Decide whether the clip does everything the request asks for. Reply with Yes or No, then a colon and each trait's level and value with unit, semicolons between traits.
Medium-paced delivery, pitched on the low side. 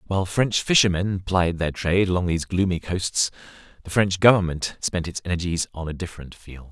Yes: average, 180 wpm; very low, 90 Hz